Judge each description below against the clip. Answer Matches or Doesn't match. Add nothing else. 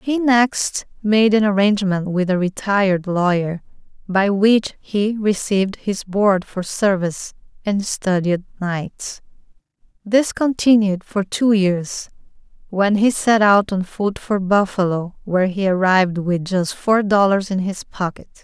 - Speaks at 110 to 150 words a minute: Matches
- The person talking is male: Doesn't match